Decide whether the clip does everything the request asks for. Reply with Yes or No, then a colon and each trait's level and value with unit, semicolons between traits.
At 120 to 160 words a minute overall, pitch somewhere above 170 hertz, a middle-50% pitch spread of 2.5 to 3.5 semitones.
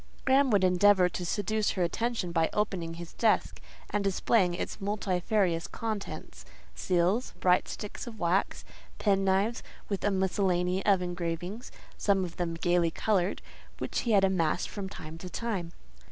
Yes: average, 145 wpm; high, 190 Hz; average, 2.8 semitones